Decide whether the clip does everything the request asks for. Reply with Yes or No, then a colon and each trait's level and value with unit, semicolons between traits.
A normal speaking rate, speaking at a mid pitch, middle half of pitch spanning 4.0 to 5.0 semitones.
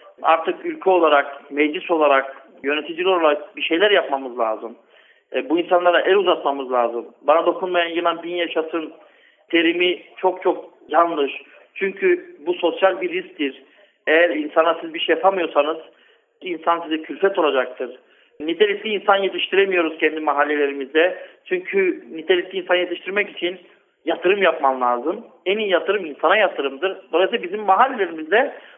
Yes: average, 125 wpm; medium, 170 Hz; average, 4.4 semitones